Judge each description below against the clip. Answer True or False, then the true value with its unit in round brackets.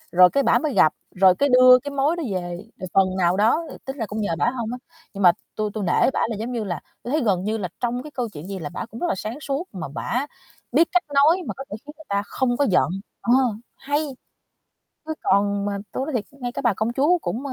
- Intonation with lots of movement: True (5.7 semitones)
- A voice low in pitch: False (235 Hz)